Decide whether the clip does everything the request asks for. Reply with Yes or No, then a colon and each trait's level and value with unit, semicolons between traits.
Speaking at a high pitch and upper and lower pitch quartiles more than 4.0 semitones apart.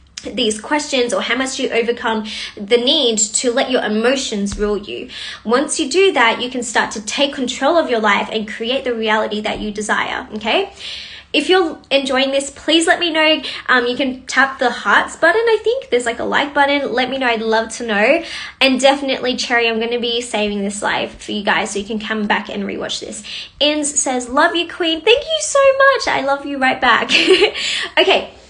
Yes: very high, 255 Hz; average, 4.6 semitones